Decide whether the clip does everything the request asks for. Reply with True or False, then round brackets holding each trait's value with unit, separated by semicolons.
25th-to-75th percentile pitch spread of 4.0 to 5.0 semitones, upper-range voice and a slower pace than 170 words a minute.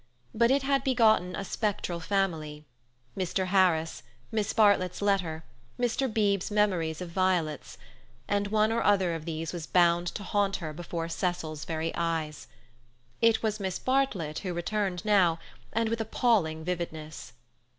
False (4.5 semitones; 180 Hz; 140 wpm)